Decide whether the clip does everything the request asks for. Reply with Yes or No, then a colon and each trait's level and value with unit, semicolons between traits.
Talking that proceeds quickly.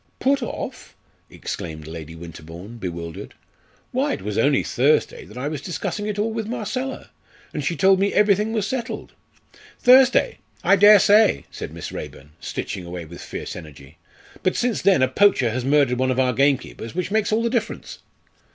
No: average, 175 wpm